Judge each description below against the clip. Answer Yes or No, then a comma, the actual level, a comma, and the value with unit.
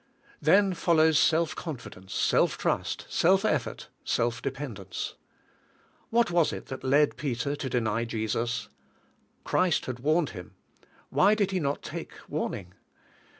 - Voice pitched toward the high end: No, medium, 140 Hz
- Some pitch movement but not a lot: No, wide, 6.5 semitones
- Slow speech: Yes, slow, 130 wpm